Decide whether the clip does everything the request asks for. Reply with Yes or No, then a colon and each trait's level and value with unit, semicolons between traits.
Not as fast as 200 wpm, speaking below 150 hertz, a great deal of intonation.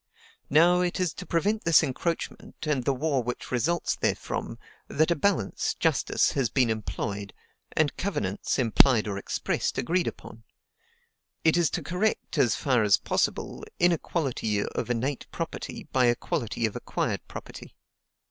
Yes: average, 145 wpm; medium, 140 Hz; wide, 6.5 semitones